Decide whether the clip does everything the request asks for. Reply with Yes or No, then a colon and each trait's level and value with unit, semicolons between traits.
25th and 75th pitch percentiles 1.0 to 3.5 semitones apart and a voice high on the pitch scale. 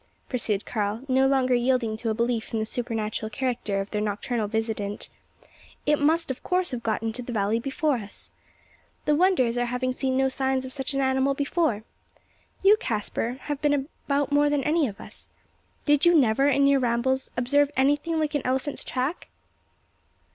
No: average, 3.9 semitones; very high, 260 Hz